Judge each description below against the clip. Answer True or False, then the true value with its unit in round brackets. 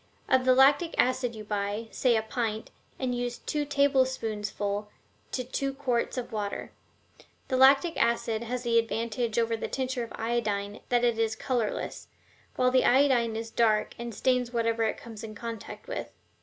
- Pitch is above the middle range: True (235 Hz)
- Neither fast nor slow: True (170 wpm)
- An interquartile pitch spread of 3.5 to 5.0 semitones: False (2.5 semitones)